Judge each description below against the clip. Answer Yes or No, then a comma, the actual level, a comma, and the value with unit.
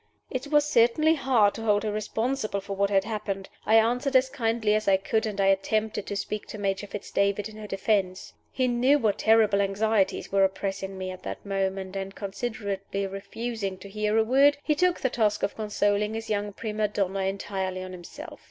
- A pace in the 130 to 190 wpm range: No, average, 200 wpm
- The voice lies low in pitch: No, high, 210 Hz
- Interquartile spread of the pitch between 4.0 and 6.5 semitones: No, narrow, 2.4 semitones